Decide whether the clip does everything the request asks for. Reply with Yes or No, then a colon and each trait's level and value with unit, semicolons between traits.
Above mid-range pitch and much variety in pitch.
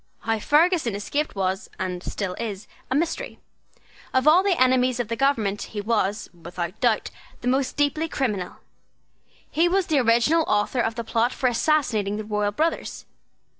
Yes: high, 235 Hz; wide, 5.9 semitones